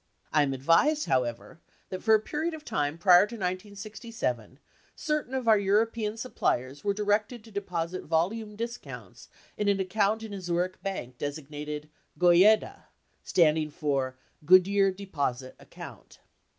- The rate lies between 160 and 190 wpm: No, average, 145 wpm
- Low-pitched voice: No, high, 190 Hz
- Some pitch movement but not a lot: No, wide, 6.0 semitones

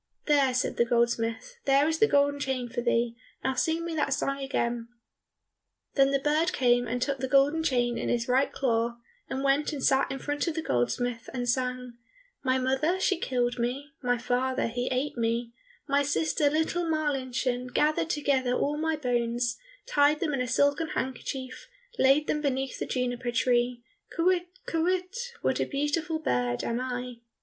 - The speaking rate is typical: Yes, average, 175 wpm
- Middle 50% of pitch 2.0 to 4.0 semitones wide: Yes, average, 3.3 semitones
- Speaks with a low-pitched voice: No, very high, 265 Hz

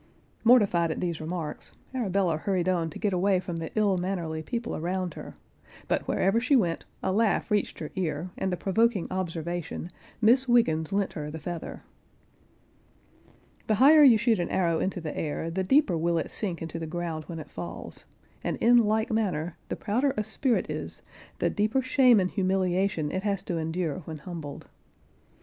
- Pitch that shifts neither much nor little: Yes, average, 4.6 semitones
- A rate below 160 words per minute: No, average, 180 wpm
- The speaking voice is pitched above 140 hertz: Yes, medium, 185 Hz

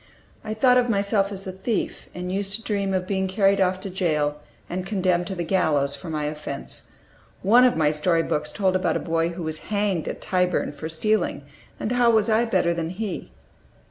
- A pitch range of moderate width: Yes, average, 3.6 semitones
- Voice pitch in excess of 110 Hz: Yes, medium, 185 Hz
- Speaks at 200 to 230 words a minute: Yes, fast, 205 wpm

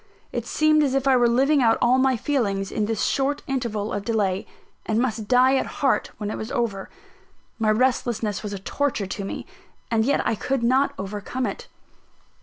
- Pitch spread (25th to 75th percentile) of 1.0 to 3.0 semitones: No, average, 4.2 semitones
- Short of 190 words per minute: No, average, 195 wpm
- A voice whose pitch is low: No, high, 235 Hz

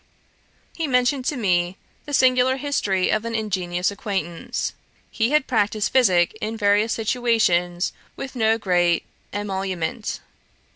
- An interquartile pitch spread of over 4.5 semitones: Yes, average, 5.2 semitones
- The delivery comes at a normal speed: No, slow, 125 wpm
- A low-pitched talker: No, high, 215 Hz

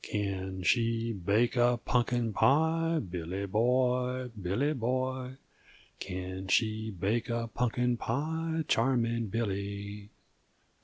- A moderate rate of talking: No, slow, 100 wpm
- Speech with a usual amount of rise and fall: Yes, average, 3.9 semitones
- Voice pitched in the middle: No, low, 115 Hz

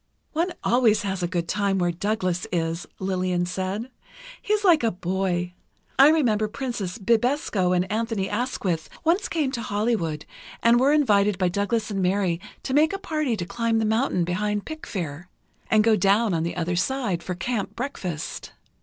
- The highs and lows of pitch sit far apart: No, average, 4.9 semitones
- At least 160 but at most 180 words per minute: Yes, average, 170 wpm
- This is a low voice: No, high, 205 Hz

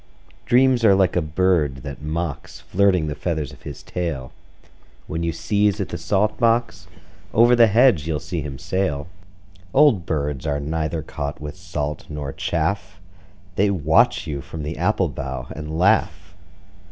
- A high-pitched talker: No, very low, 85 Hz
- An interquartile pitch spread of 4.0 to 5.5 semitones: Yes, average, 4.7 semitones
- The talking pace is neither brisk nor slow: Yes, average, 160 wpm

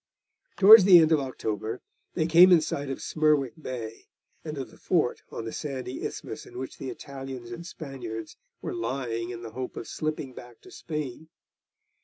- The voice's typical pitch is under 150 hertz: Yes, low, 135 Hz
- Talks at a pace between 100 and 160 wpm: No, average, 180 wpm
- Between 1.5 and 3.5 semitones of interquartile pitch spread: No, average, 4.5 semitones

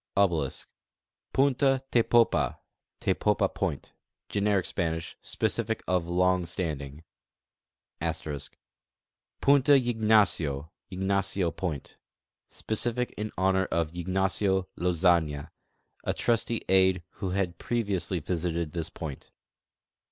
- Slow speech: Yes, slow, 95 wpm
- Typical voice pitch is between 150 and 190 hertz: No, very low, 95 Hz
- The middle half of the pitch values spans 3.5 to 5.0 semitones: Yes, average, 4.0 semitones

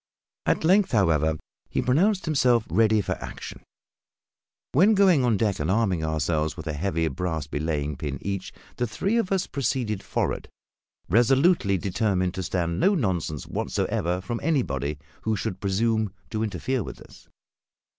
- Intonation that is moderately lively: No, wide, 7.4 semitones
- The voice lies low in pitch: Yes, low, 100 Hz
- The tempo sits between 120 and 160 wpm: Yes, average, 150 wpm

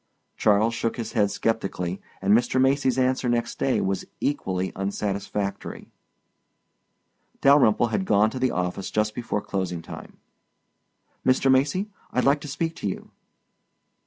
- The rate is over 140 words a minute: No, slow, 135 wpm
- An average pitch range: Yes, average, 4.7 semitones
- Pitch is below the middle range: Yes, low, 115 Hz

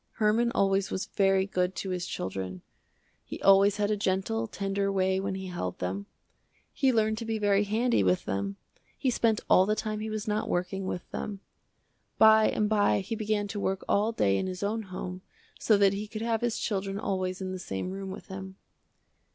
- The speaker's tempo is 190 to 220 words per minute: Yes, average, 200 wpm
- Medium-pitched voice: No, high, 195 Hz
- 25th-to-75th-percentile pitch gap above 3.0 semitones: No, narrow, 2.4 semitones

